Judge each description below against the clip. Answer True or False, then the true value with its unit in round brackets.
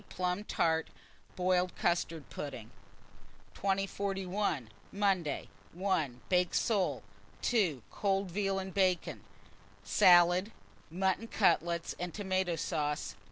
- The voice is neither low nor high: True (180 Hz)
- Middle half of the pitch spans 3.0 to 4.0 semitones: False (2.6 semitones)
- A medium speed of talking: False (95 wpm)